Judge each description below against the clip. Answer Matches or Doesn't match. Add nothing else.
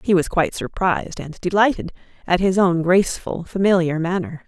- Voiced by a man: Doesn't match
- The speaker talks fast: Doesn't match